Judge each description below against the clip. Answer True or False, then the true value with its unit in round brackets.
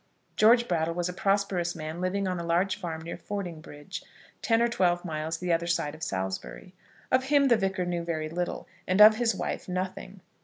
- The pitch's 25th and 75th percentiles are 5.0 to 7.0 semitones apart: False (3.1 semitones)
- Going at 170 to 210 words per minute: True (195 wpm)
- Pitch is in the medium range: True (180 Hz)